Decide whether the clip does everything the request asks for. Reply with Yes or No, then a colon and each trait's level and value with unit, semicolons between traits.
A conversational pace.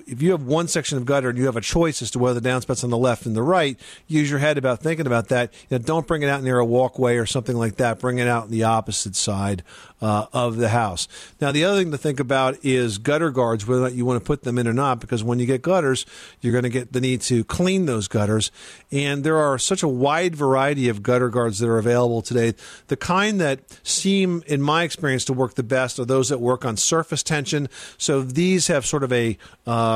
No: fast, 255 wpm